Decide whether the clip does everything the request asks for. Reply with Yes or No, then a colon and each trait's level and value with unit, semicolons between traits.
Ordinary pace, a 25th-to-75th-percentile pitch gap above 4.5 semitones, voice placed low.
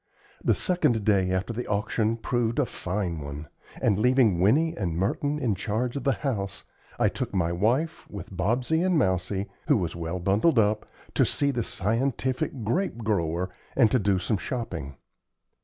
Yes: average, 170 wpm; average, 5.3 semitones; low, 105 Hz